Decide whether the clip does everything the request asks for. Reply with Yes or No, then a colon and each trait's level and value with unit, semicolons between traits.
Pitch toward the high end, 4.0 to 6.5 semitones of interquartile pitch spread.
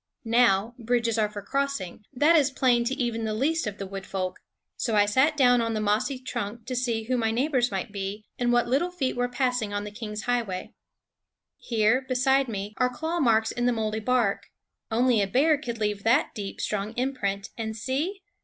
No: high, 235 Hz; average, 3.5 semitones